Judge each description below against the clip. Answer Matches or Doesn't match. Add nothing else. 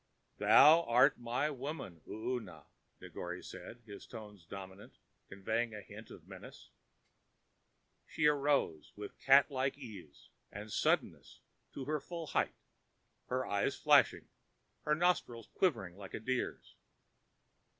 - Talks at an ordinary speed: Doesn't match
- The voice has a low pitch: Matches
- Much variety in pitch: Matches